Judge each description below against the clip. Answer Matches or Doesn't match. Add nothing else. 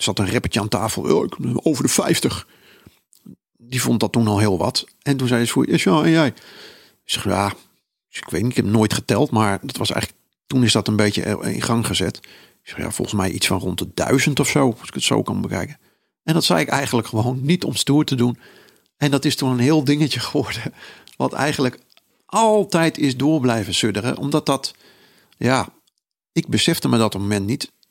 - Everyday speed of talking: Doesn't match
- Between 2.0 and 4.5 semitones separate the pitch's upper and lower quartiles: Doesn't match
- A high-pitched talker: Doesn't match